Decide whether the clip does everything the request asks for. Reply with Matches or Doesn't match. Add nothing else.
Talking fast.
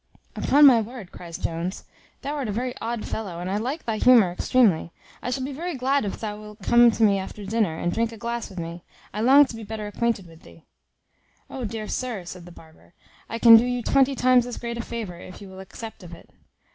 Matches